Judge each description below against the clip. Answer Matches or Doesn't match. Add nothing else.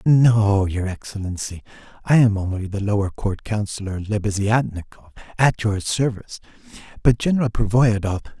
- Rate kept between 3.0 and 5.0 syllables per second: Doesn't match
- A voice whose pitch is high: Doesn't match